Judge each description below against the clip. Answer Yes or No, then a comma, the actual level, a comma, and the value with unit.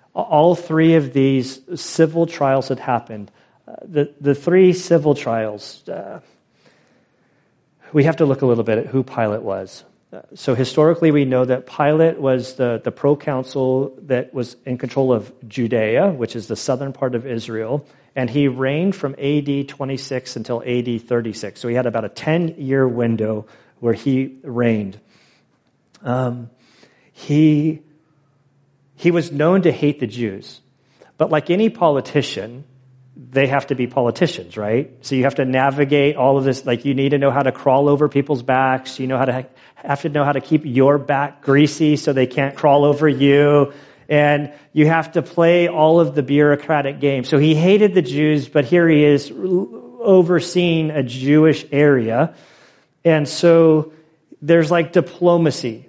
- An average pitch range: Yes, average, 3.1 semitones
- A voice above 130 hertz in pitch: Yes, medium, 140 Hz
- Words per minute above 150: Yes, average, 165 wpm